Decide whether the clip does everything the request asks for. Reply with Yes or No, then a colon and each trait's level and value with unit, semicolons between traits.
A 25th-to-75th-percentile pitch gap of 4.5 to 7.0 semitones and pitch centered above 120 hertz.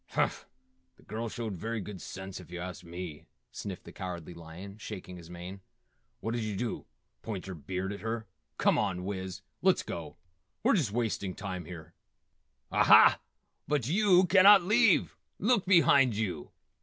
No: average, 5.2 semitones; low, 100 Hz